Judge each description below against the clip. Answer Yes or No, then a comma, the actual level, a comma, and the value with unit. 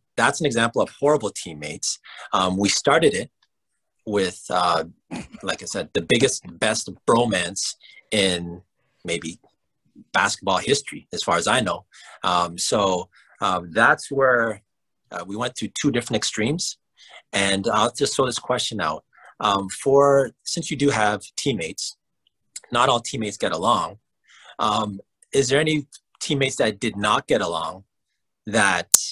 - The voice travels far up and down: Yes, wide, 6.2 semitones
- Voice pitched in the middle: No, low, 110 Hz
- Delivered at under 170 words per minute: Yes, average, 145 wpm